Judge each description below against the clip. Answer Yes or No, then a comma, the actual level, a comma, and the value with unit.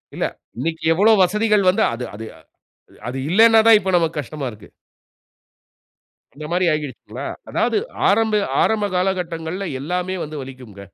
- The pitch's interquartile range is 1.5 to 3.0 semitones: No, average, 5.2 semitones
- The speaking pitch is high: No, medium, 175 Hz